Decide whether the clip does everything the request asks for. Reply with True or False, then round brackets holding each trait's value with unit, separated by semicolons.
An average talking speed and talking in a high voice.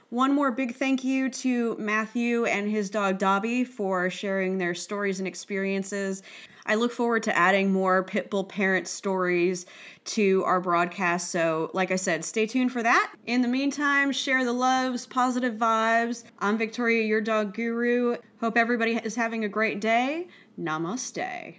True (160 wpm; 220 Hz)